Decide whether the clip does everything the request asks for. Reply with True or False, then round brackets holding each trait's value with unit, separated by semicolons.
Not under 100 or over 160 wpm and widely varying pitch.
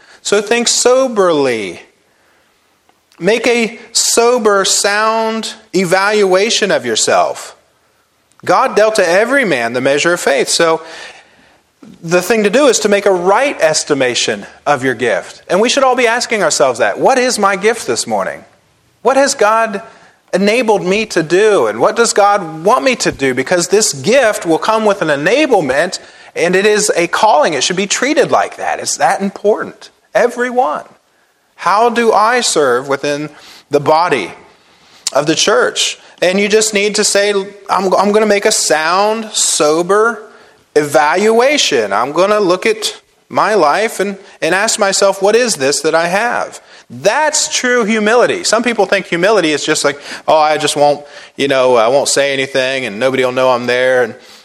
False (170 wpm; 5.7 semitones)